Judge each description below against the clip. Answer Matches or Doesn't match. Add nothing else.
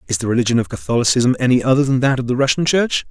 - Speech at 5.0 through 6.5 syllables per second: Doesn't match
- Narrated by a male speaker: Matches